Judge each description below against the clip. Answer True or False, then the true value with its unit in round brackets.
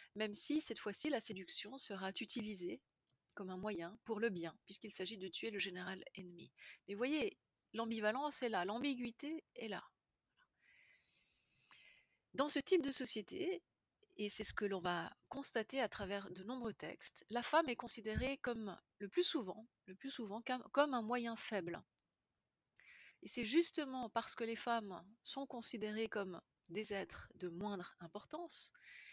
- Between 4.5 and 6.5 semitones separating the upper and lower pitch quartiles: True (5.1 semitones)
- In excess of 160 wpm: False (155 wpm)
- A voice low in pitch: False (225 Hz)